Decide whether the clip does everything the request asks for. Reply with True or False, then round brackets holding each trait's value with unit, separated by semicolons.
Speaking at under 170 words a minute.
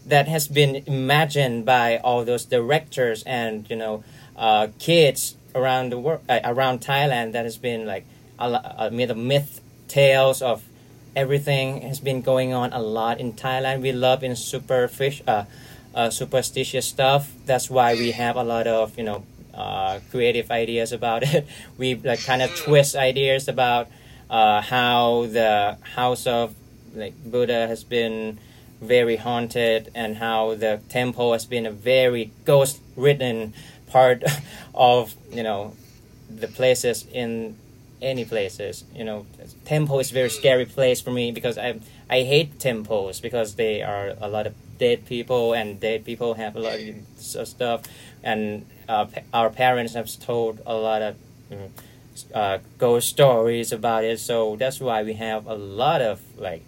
True (160 wpm)